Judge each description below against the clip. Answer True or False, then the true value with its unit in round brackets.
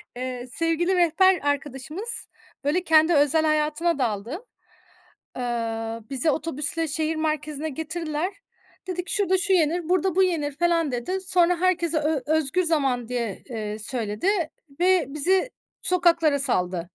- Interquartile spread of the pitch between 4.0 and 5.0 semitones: True (4.6 semitones)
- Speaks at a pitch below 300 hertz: False (310 Hz)